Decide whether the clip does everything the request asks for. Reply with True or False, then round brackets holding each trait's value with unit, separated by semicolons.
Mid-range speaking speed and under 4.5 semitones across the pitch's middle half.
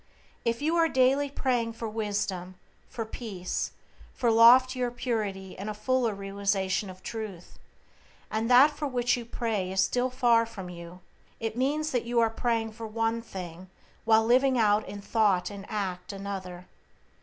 True (160 wpm; 3.8 semitones)